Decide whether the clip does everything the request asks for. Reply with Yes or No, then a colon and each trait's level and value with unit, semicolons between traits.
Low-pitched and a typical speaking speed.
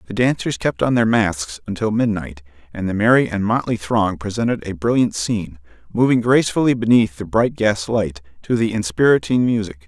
Yes: low, 105 Hz; average, 175 wpm